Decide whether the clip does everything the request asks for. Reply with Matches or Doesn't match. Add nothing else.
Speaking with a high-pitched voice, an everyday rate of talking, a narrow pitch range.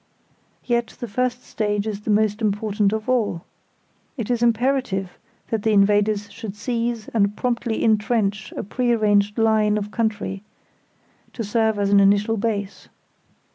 Matches